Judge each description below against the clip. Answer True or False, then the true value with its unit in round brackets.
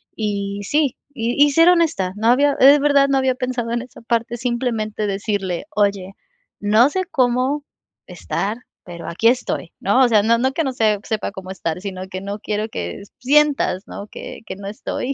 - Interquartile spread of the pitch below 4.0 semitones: False (4.6 semitones)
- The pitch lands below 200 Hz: False (230 Hz)